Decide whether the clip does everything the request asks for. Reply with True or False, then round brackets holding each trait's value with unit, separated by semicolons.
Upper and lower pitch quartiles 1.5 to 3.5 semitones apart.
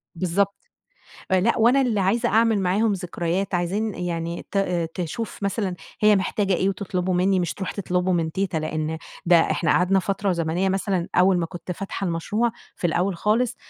True (2.5 semitones)